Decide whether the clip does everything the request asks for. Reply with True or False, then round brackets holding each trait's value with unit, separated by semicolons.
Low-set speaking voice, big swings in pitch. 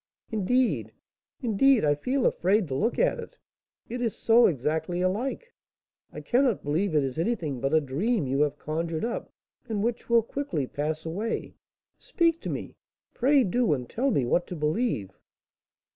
False (195 Hz; 8.0 semitones)